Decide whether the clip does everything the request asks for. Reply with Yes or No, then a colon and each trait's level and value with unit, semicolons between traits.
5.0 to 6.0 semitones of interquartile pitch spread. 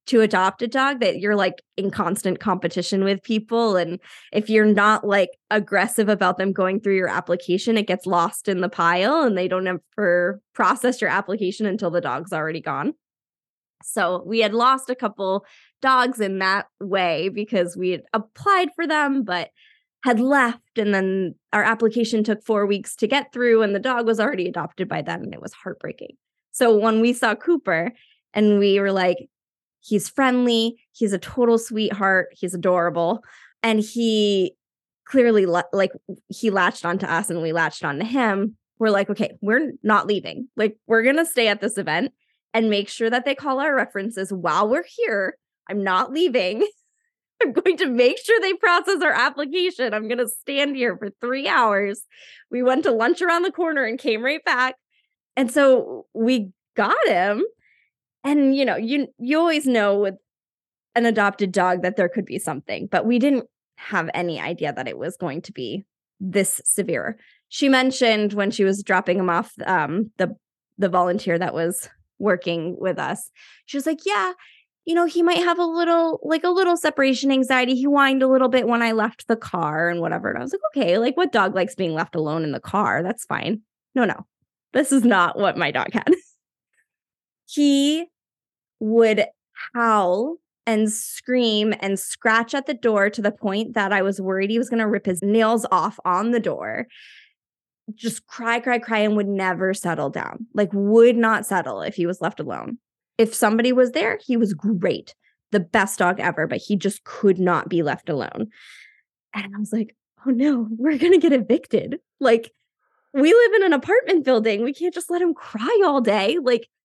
Yes: wide, 5.4 semitones